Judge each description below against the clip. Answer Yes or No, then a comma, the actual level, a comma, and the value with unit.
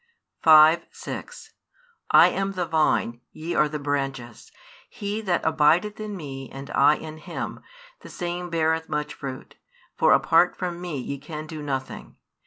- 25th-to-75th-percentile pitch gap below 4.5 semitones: Yes, average, 3.6 semitones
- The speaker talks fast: No, average, 155 wpm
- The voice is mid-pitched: Yes, medium, 155 Hz